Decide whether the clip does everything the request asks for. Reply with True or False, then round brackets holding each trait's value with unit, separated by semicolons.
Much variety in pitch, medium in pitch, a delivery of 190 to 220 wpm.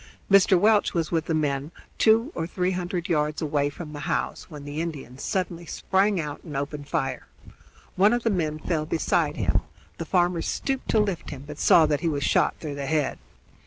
False (3.7 semitones; 160 Hz; 200 wpm)